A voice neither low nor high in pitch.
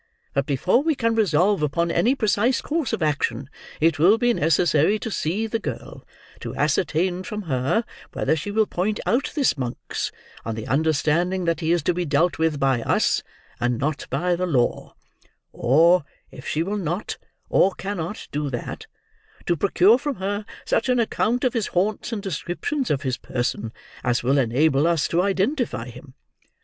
Yes: medium, 175 Hz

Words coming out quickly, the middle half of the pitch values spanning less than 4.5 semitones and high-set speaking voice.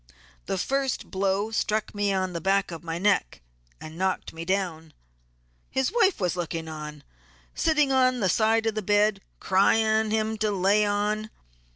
No: average, 170 wpm; average, 3.3 semitones; high, 205 Hz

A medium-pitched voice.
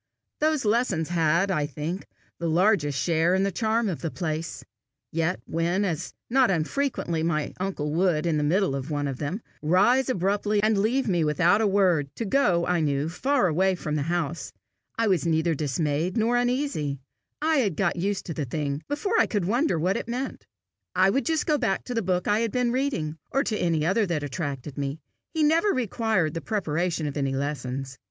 Yes: medium, 180 Hz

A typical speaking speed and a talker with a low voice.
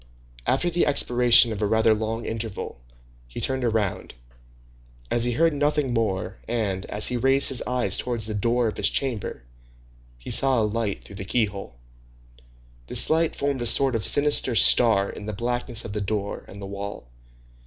Yes: average, 175 wpm; low, 115 Hz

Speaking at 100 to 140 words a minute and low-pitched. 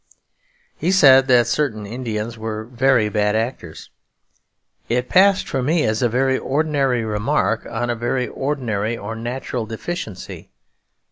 Yes: slow, 135 wpm; low, 120 Hz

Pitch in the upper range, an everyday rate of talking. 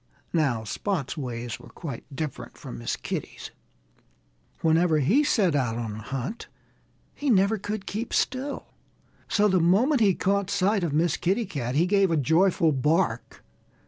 No: medium, 170 Hz; average, 155 wpm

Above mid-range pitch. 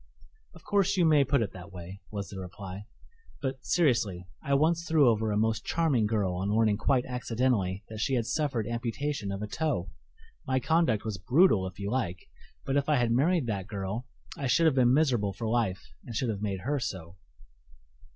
No: low, 115 Hz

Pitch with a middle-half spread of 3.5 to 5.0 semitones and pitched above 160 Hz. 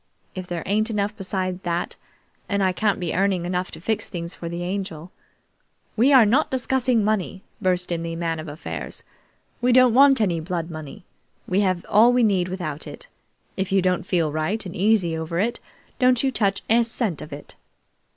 Yes: average, 4.2 semitones; medium, 185 Hz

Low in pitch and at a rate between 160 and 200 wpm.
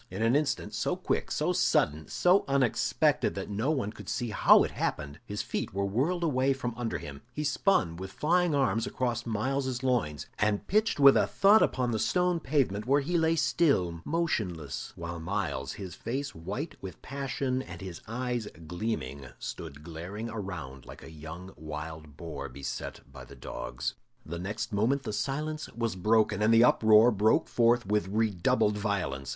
Yes: low, 110 Hz; average, 175 wpm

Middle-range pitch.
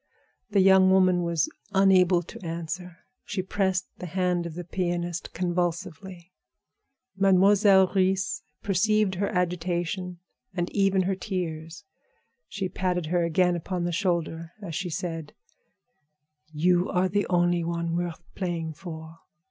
Yes: medium, 180 Hz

